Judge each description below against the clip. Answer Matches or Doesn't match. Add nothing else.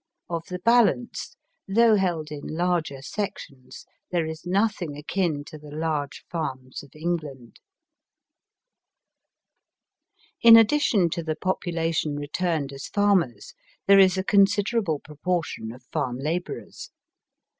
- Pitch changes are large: Doesn't match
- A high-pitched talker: Doesn't match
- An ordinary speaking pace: Doesn't match